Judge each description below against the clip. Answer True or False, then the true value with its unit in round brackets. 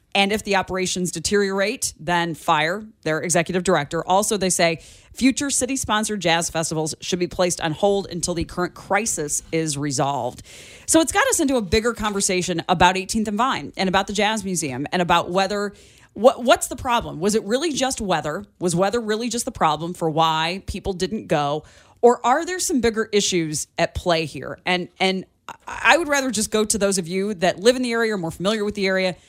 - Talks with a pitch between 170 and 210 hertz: True (190 Hz)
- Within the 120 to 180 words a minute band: False (205 wpm)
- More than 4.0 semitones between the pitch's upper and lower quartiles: True (4.6 semitones)